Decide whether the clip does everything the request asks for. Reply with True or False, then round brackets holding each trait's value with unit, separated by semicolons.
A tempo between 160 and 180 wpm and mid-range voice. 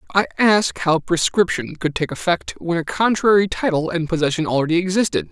True (170 wpm; 175 Hz)